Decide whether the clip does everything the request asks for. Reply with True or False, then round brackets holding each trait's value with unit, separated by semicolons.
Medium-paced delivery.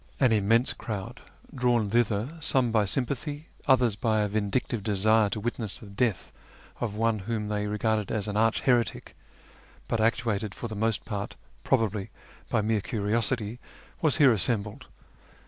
True (150 wpm)